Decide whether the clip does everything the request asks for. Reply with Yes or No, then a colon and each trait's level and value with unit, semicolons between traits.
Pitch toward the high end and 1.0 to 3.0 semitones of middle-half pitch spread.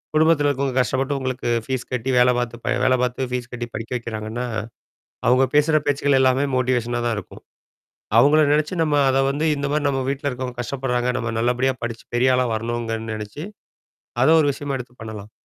No: low, 125 Hz; narrow, 2.6 semitones